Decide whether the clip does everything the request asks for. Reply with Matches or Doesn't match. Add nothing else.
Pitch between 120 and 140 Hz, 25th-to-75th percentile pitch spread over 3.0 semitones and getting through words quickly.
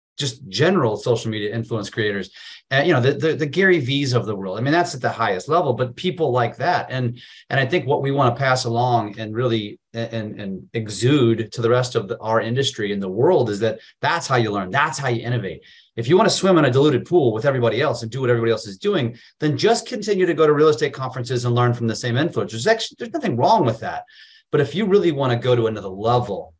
Matches